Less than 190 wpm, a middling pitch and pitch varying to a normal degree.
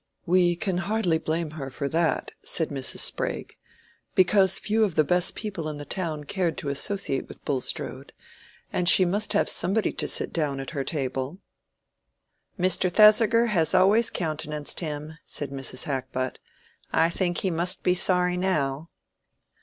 Yes: average, 155 wpm; medium, 170 Hz; average, 4.2 semitones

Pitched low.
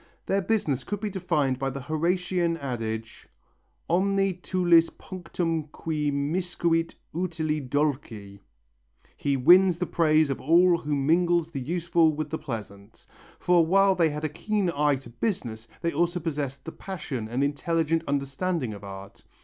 No: medium, 160 Hz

